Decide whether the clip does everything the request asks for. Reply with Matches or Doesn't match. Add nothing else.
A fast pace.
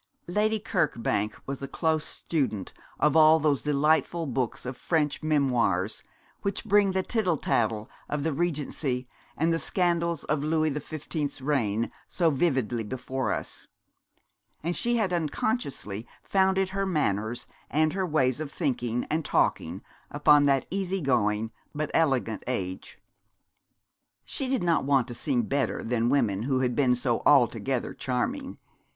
Doesn't match